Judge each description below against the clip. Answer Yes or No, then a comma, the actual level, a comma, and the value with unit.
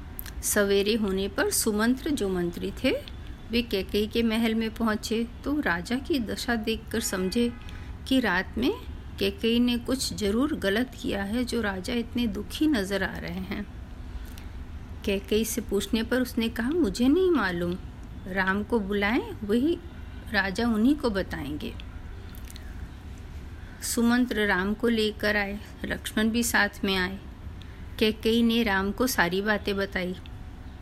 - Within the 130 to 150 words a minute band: Yes, average, 140 wpm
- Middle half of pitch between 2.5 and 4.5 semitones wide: No, average, 5.2 semitones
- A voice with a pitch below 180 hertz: No, high, 210 Hz